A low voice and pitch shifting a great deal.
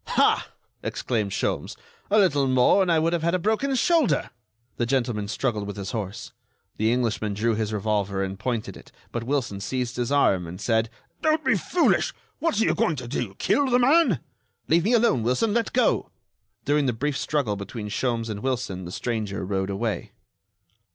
Yes: low, 120 Hz; wide, 7.7 semitones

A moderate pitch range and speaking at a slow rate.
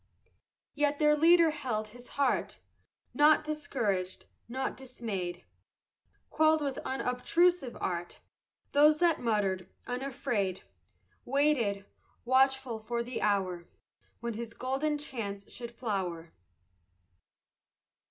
No: wide, 6.0 semitones; slow, 95 wpm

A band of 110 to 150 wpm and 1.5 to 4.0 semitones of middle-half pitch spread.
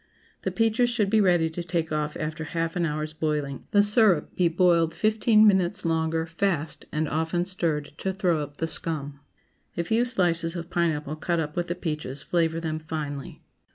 No: average, 185 wpm; average, 2.8 semitones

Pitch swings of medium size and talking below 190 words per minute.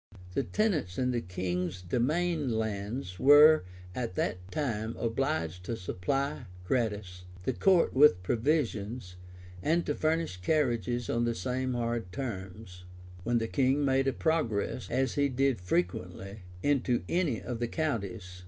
No: wide, 6.7 semitones; average, 140 wpm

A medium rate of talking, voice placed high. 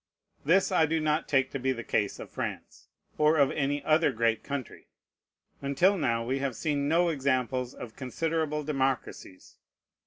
No: average, 160 wpm; medium, 140 Hz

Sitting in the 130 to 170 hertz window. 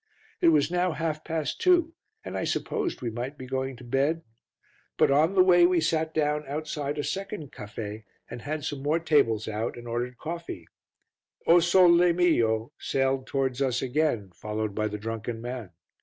Yes: medium, 140 Hz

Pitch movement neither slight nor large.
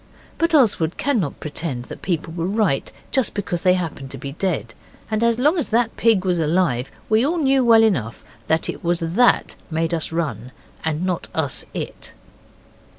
No: wide, 6.2 semitones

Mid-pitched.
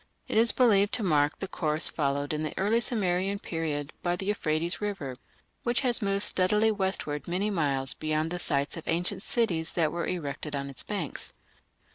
Yes: medium, 175 Hz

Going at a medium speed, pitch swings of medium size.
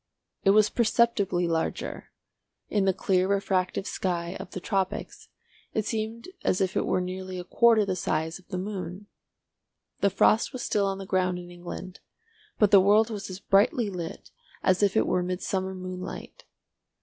No: average, 170 wpm; narrow, 2.1 semitones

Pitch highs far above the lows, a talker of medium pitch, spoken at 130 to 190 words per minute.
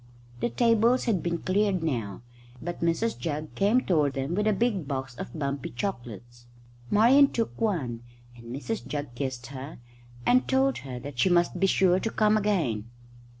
Yes: wide, 8.3 semitones; medium, 170 Hz; average, 170 wpm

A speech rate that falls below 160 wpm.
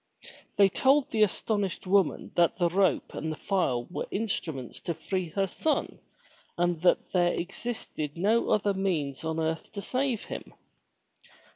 Yes: average, 150 wpm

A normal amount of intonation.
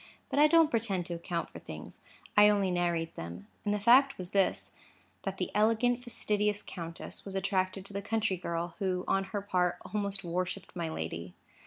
Yes: average, 3.0 semitones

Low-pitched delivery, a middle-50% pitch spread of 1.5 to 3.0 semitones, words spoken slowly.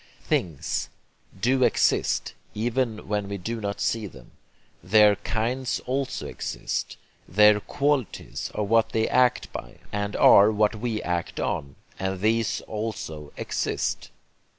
Yes: low, 105 Hz; narrow, 2.5 semitones; slow, 130 wpm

